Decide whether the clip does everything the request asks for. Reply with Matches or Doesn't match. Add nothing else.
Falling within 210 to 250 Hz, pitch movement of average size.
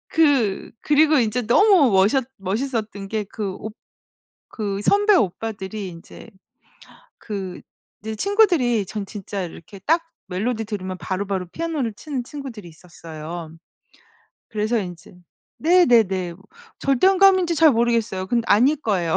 Doesn't match